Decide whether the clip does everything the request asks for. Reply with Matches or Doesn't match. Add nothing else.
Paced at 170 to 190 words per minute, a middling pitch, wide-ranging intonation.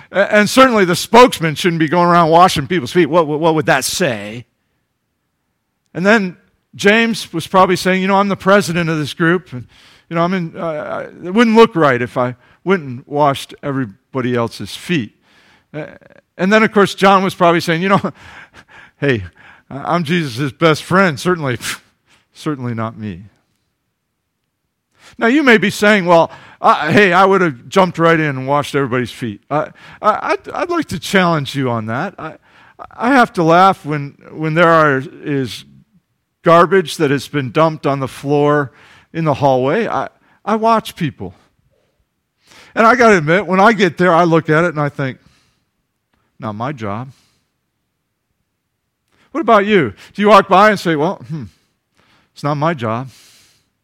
Matches